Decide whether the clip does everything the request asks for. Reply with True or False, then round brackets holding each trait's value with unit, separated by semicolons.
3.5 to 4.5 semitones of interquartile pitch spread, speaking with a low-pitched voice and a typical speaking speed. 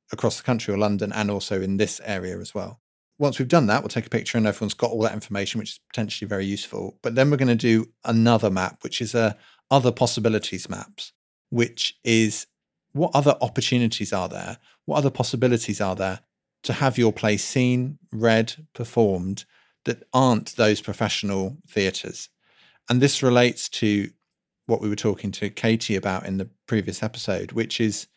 False (2.9 semitones; 110 Hz; 185 wpm)